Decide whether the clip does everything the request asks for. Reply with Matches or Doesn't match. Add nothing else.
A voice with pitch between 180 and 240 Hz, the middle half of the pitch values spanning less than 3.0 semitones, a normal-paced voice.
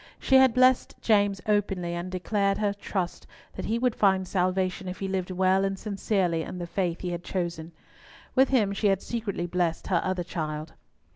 Matches